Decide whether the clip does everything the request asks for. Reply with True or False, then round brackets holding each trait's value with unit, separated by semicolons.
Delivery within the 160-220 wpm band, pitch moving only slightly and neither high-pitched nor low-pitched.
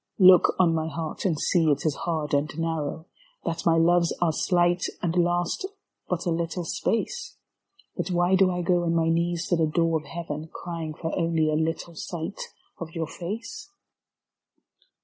True (180 wpm; 1.5 semitones; 165 Hz)